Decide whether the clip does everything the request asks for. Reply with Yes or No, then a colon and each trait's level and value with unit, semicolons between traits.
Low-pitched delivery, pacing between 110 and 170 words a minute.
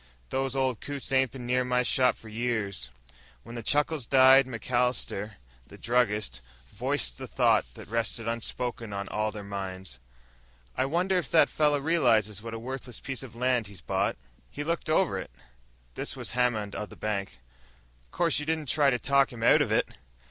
No: low, 125 Hz; average, 180 wpm